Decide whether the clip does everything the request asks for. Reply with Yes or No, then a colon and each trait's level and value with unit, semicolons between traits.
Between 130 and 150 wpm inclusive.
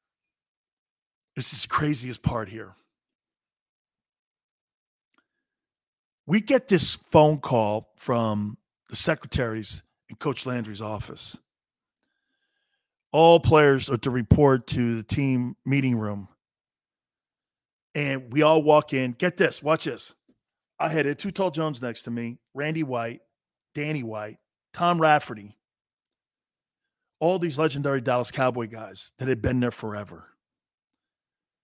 No: slow, 120 wpm